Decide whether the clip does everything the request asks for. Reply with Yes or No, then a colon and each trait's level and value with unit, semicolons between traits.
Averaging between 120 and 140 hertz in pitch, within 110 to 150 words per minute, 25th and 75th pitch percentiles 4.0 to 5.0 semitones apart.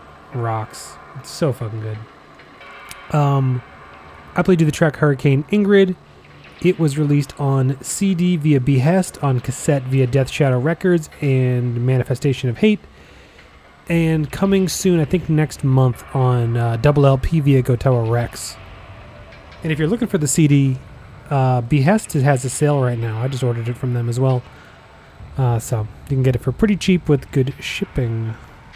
No: low, 135 Hz; average, 165 wpm; average, 4.5 semitones